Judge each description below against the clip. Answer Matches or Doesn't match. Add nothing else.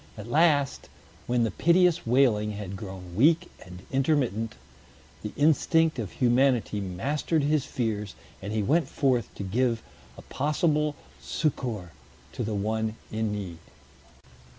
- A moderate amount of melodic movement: Doesn't match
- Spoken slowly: Matches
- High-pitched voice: Doesn't match